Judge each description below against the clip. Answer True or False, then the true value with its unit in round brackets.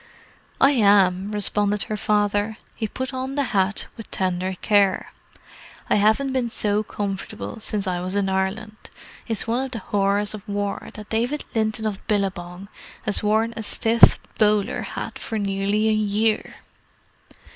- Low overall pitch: False (210 Hz)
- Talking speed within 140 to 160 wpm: True (155 wpm)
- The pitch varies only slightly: True (1.9 semitones)